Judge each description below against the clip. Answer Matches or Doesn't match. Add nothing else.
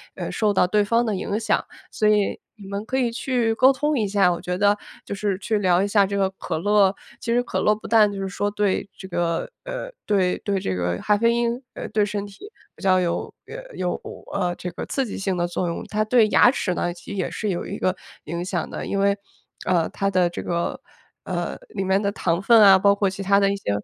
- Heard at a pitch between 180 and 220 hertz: Matches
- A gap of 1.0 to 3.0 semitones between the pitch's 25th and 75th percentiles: Matches